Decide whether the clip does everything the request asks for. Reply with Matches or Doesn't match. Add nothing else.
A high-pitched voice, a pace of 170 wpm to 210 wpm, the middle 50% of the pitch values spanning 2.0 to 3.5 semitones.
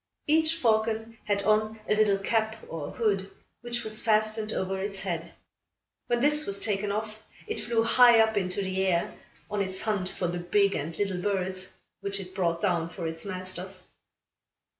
Matches